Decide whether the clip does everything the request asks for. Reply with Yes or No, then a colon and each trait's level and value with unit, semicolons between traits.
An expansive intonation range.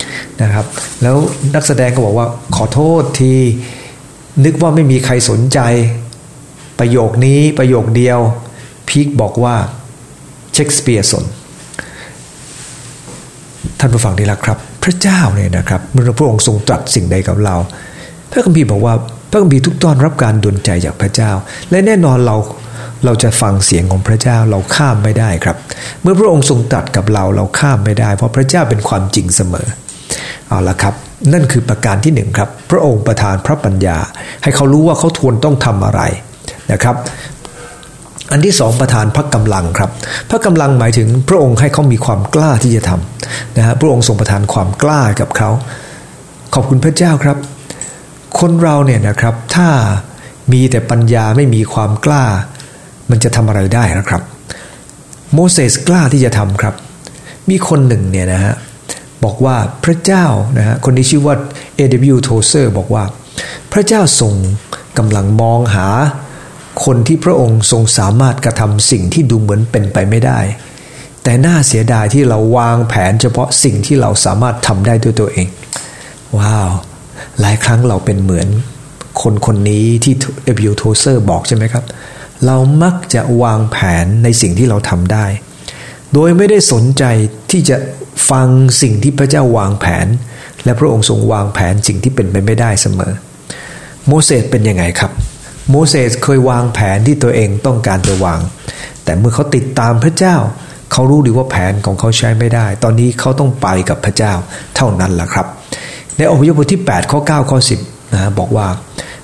No: average, 4.6 semitones